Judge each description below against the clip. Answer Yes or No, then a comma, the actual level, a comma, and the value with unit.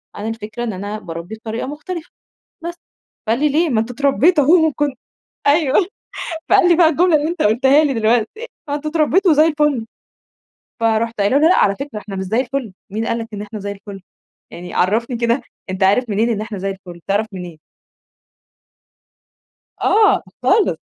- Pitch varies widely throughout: Yes, wide, 6.3 semitones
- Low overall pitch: No, high, 235 Hz